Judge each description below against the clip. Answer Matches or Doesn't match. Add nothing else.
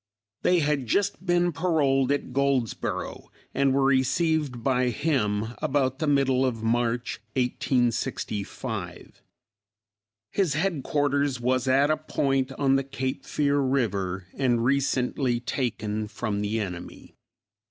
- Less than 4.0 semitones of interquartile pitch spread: Matches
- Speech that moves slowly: Matches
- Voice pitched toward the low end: Matches